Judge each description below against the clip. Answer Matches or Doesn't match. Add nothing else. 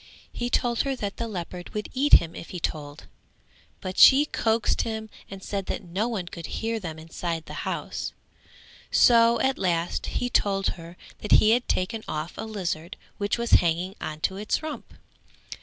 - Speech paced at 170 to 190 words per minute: Matches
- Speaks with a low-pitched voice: Doesn't match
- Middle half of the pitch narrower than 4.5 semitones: Doesn't match